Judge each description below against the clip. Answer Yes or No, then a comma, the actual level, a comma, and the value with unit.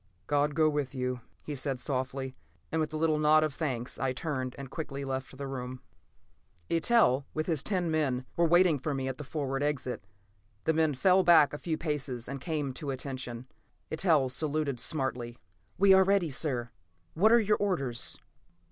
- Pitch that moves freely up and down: No, average, 3.5 semitones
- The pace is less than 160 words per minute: No, average, 180 wpm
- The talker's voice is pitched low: No, medium, 145 Hz